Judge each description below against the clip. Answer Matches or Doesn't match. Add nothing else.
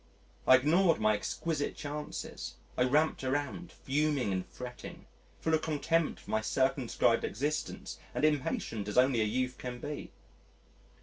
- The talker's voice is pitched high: Doesn't match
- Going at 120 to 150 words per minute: Matches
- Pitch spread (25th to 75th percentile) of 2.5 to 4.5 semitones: Matches